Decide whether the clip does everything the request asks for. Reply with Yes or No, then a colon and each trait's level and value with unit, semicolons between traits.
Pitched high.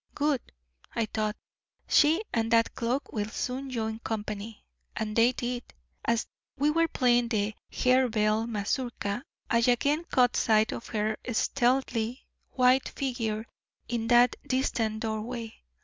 Yes: high, 235 Hz